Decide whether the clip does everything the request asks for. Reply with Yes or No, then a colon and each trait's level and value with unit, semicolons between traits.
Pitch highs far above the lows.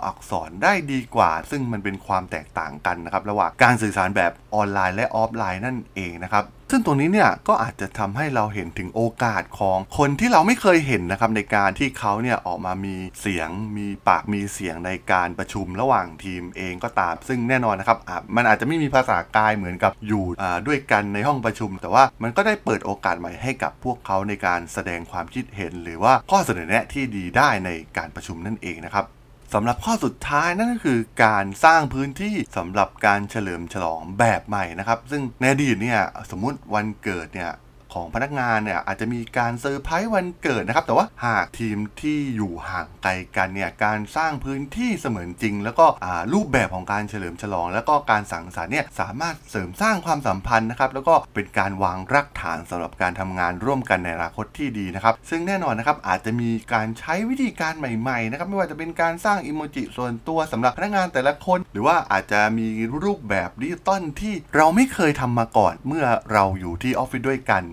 Yes: wide, 6.1 semitones